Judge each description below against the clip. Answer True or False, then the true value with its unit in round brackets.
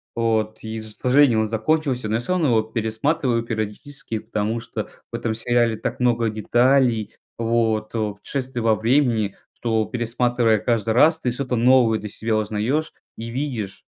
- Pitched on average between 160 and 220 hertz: False (115 Hz)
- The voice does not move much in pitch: True (2.3 semitones)